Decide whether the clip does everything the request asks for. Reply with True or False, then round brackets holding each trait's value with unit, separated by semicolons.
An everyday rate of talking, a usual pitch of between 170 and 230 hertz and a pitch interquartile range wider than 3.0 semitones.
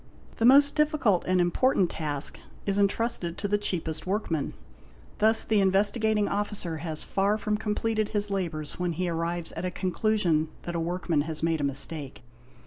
True (165 wpm; 185 Hz; 4.2 semitones)